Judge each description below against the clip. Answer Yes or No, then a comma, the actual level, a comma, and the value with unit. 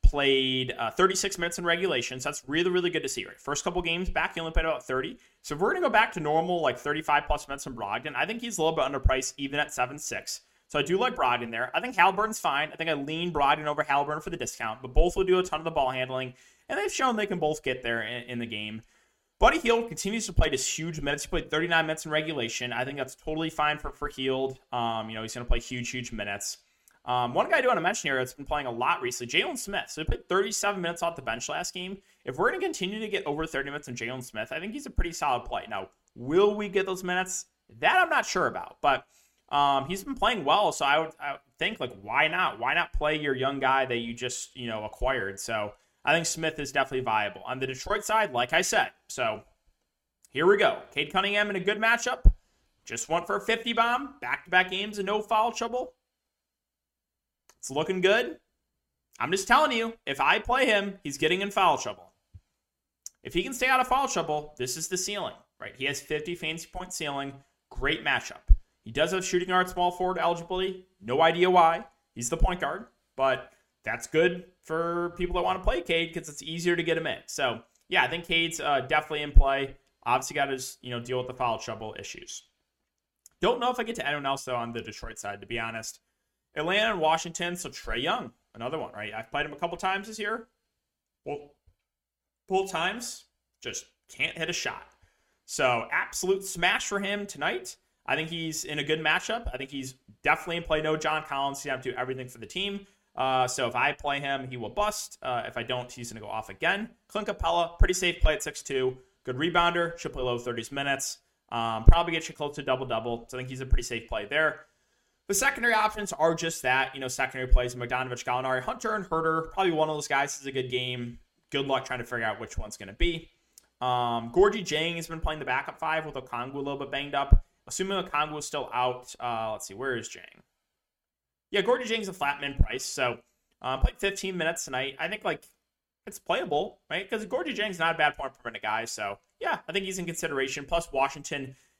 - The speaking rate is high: Yes, fast, 235 wpm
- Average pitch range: No, wide, 6.2 semitones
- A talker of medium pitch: Yes, medium, 150 Hz